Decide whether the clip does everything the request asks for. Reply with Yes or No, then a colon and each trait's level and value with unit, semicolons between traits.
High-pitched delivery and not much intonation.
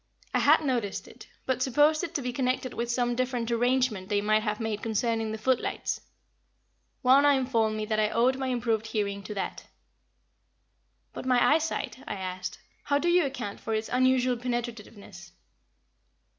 No: high, 240 Hz; average, 3.2 semitones